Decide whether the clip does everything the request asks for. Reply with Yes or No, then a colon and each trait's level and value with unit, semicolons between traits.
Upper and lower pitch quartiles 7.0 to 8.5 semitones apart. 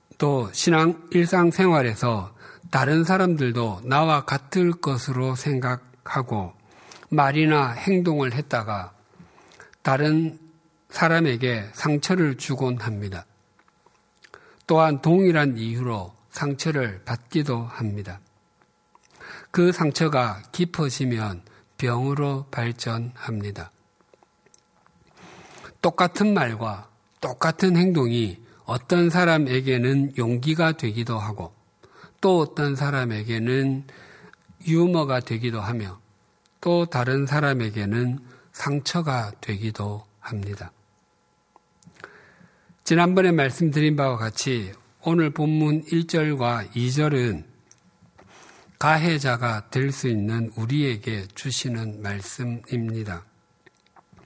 No: wide, 5.6 semitones